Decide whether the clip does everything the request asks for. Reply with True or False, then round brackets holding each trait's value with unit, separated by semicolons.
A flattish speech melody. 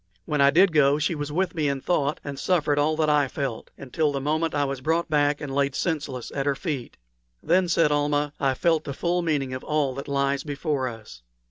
True (2.2 semitones)